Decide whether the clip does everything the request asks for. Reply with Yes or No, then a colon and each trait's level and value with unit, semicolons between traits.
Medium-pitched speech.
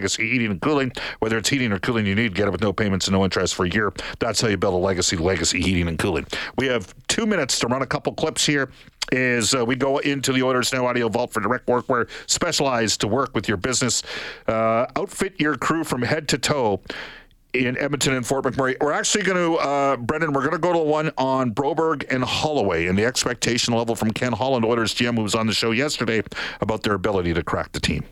No: low, 125 Hz